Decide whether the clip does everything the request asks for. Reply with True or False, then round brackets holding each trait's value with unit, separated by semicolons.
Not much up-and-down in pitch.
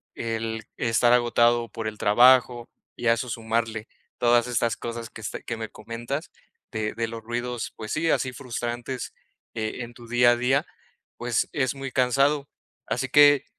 True (1.6 semitones)